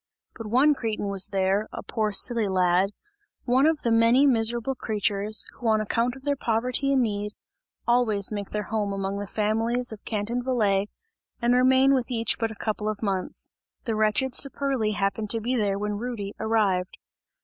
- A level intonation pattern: No, average, 3.2 semitones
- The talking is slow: No, average, 180 wpm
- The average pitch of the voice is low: No, high, 220 Hz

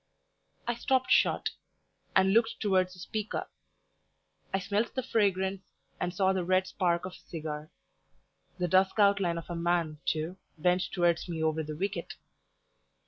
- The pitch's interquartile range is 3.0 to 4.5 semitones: No, narrow, 2.5 semitones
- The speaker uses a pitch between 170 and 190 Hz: Yes, medium, 185 Hz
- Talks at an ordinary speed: Yes, average, 150 wpm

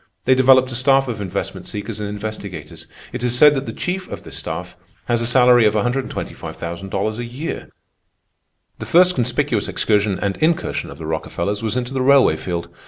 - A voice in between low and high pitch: No, low, 120 Hz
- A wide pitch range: No, average, 4.3 semitones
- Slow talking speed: No, average, 180 wpm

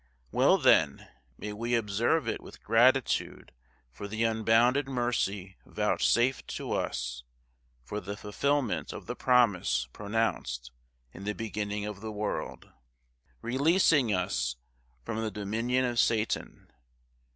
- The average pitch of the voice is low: Yes, low, 110 Hz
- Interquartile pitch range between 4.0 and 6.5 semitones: No, average, 3.1 semitones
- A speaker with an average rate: No, slow, 120 wpm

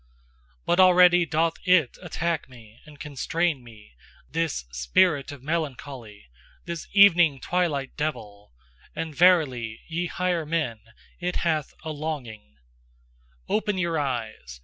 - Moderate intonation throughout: No, wide, 5.7 semitones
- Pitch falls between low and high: Yes, medium, 155 Hz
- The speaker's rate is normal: No, slow, 120 wpm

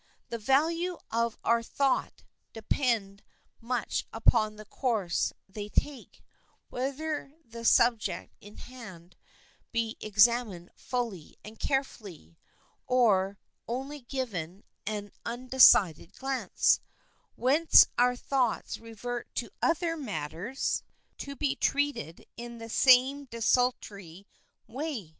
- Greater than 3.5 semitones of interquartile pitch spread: Yes, average, 4.3 semitones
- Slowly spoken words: Yes, slow, 100 wpm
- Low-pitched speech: No, high, 235 Hz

